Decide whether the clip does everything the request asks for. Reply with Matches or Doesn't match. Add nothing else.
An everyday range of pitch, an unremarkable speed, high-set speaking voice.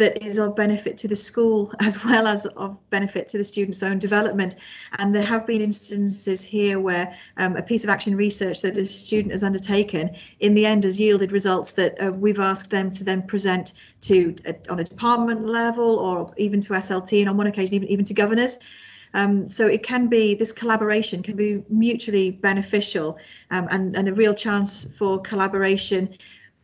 Doesn't match